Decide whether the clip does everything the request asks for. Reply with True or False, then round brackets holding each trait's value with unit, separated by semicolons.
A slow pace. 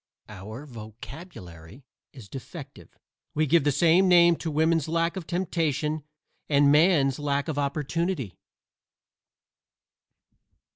True (105 wpm)